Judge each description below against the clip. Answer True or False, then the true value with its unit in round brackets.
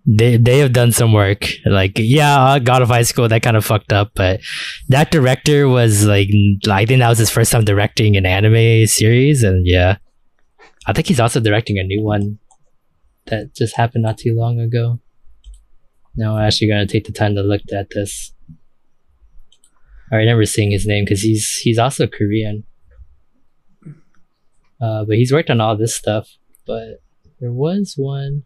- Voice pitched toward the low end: True (110 Hz)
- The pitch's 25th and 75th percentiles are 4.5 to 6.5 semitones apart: False (2.9 semitones)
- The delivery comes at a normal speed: True (175 wpm)